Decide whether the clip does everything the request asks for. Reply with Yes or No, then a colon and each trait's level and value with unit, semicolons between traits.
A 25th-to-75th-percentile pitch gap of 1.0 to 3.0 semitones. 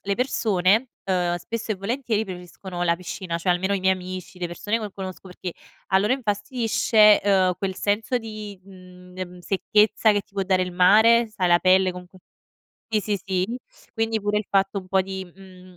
Yes: narrow, 2.5 semitones